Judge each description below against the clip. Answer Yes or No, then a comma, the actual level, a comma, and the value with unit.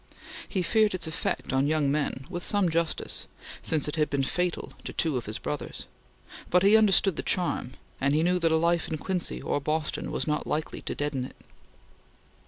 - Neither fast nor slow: Yes, average, 195 wpm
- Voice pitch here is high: No, medium, 160 Hz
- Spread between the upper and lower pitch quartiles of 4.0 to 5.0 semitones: No, average, 3.5 semitones